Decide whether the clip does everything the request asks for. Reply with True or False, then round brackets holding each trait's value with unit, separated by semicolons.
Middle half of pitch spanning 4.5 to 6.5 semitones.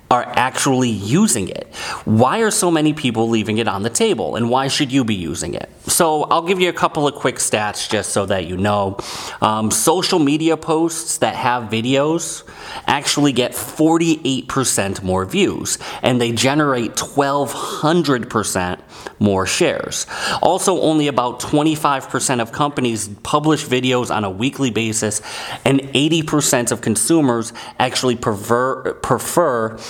True (5.2 semitones)